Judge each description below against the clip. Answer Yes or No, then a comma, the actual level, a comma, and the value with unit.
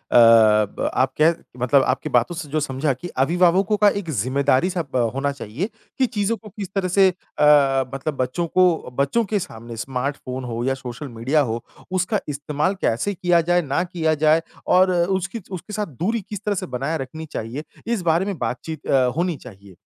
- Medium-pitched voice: Yes, medium, 155 Hz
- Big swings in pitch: Yes, wide, 6.1 semitones